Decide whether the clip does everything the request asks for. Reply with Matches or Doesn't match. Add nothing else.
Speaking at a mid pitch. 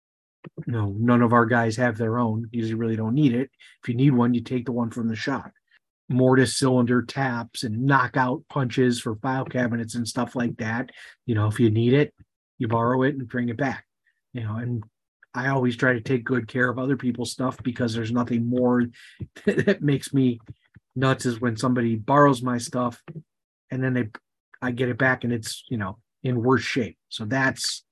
Doesn't match